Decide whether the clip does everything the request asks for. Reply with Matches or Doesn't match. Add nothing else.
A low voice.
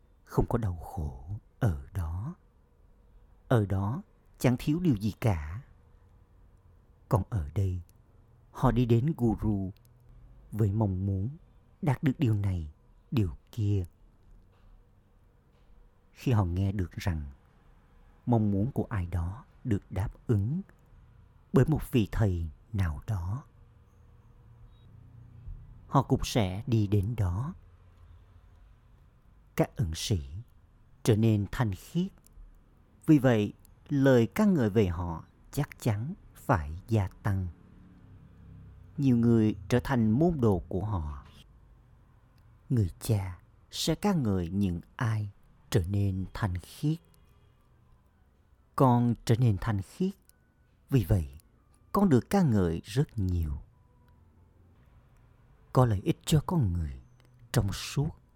Matches